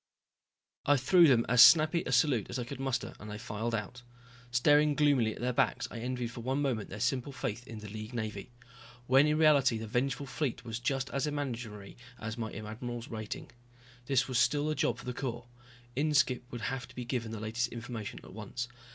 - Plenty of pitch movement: No, average, 3.3 semitones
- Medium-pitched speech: No, low, 125 Hz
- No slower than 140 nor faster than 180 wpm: No, fast, 205 wpm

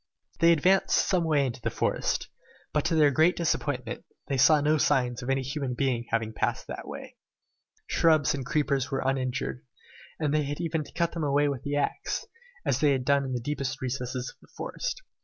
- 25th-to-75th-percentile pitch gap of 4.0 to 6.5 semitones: No, average, 3.0 semitones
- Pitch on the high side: No, medium, 140 Hz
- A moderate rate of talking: No, fast, 210 wpm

